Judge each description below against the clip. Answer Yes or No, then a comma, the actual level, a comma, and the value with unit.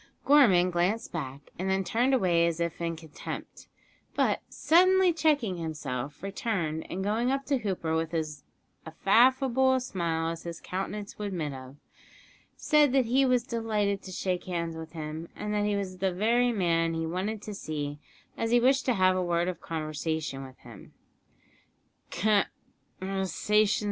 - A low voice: No, medium, 185 Hz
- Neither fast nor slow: Yes, average, 160 wpm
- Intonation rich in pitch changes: Yes, wide, 6.0 semitones